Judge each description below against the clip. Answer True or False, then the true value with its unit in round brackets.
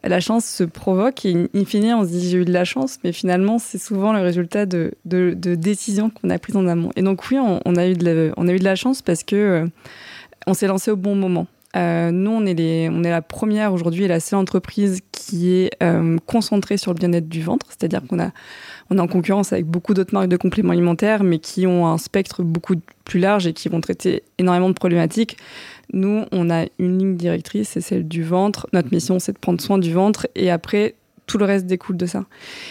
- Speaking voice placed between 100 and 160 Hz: False (185 Hz)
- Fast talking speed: True (240 wpm)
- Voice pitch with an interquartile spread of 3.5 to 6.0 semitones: False (2.7 semitones)